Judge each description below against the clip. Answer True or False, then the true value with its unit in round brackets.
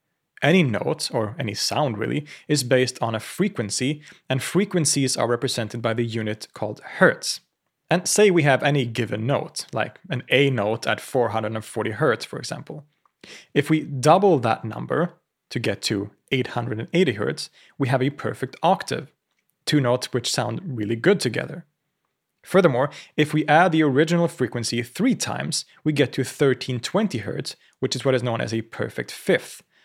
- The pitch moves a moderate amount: True (4.4 semitones)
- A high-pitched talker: False (130 Hz)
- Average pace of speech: True (165 wpm)